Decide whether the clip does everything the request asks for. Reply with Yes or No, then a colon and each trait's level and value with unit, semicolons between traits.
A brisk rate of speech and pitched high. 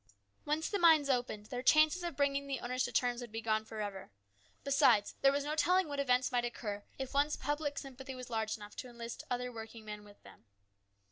Yes: fast, 220 wpm; very high, 250 Hz